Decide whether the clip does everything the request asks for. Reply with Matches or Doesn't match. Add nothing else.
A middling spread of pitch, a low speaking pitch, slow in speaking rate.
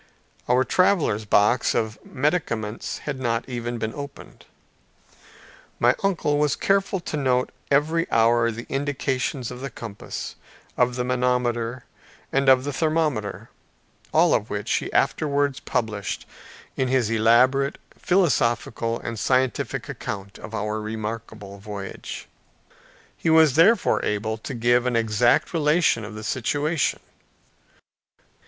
Matches